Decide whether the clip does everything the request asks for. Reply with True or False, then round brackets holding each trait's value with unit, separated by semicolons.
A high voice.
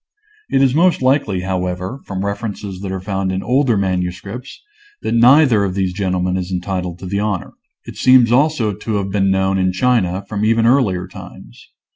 False (100 Hz)